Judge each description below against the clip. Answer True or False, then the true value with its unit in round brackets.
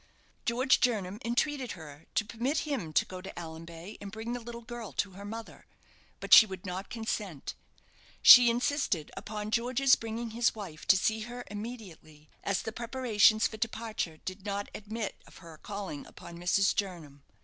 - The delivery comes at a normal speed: True (170 wpm)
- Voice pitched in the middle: False (215 Hz)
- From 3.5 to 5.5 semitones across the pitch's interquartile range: True (4.3 semitones)